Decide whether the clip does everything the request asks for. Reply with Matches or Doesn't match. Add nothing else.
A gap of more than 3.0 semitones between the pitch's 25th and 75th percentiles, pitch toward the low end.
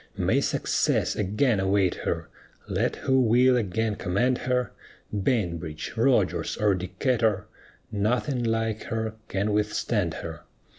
Matches